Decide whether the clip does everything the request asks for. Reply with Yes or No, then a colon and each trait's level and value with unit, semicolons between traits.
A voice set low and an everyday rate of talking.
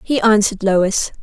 No: high, 205 Hz; average, 145 wpm